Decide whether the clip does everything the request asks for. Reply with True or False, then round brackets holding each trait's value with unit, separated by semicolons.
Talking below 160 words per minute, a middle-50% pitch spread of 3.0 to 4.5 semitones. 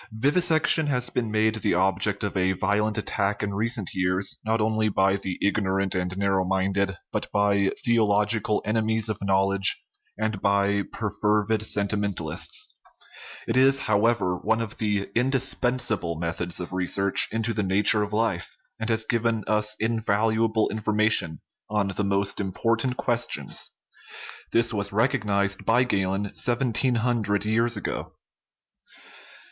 False (140 wpm; 2.4 semitones)